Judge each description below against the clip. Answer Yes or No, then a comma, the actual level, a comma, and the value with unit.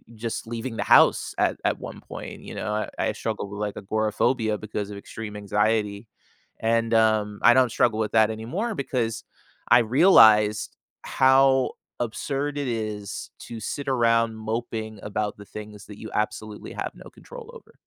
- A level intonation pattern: Yes, narrow, 2.3 semitones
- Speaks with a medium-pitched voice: No, low, 110 Hz